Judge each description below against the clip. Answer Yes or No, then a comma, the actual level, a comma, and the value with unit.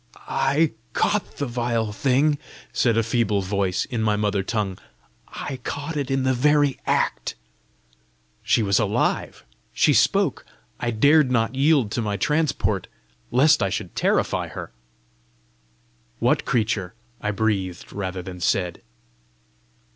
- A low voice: Yes, low, 115 Hz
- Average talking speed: No, slow, 130 wpm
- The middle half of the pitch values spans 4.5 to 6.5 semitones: Yes, average, 5.2 semitones